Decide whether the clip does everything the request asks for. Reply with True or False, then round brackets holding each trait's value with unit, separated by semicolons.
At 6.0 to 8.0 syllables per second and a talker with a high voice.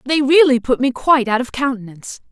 True (6.1 syllables/s; 260 Hz)